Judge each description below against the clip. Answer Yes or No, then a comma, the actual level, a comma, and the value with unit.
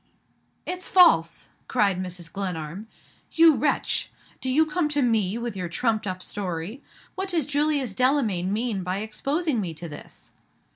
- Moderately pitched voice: No, high, 220 Hz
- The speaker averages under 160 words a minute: Yes, average, 150 wpm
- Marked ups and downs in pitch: Yes, wide, 7.9 semitones